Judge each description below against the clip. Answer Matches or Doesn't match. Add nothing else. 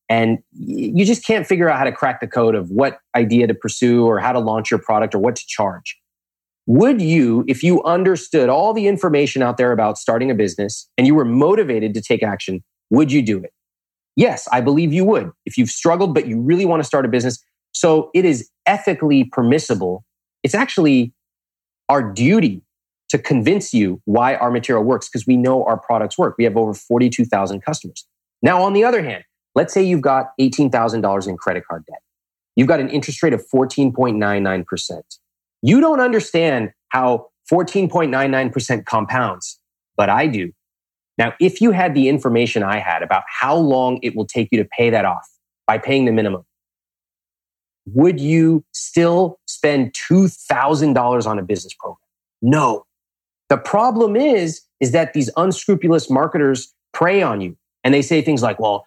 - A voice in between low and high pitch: Doesn't match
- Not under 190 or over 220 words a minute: Doesn't match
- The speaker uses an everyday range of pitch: Doesn't match